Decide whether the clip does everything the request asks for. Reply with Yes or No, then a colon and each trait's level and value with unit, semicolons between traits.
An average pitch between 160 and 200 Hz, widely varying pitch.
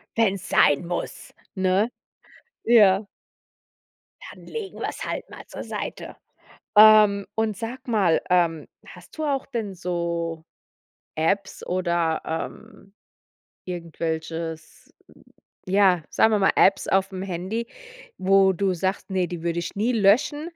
No: high, 190 Hz; average, 3.9 semitones